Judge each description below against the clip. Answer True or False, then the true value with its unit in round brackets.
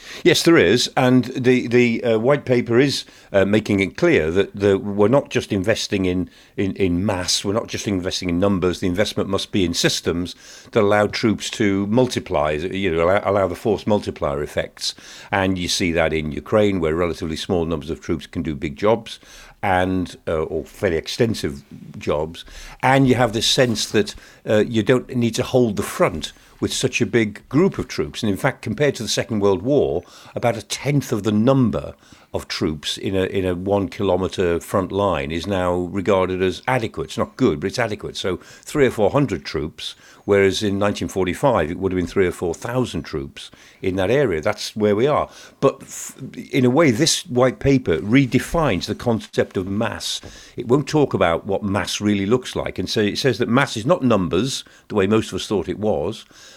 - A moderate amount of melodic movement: True (4.9 semitones)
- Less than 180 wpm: False (205 wpm)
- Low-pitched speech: True (105 Hz)